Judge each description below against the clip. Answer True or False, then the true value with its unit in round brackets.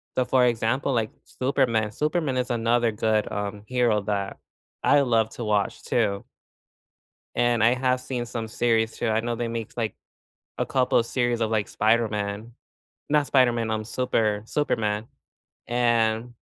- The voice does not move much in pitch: True (2.2 semitones)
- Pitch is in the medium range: False (115 Hz)